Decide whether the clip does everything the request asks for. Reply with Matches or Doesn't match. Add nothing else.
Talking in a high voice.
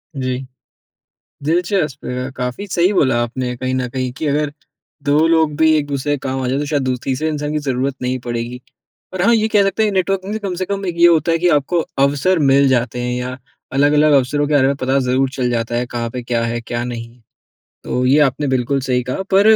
Doesn't match